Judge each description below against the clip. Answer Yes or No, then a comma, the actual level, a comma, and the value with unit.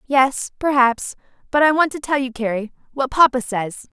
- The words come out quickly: No, average, 165 wpm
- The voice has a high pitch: Yes, very high, 260 Hz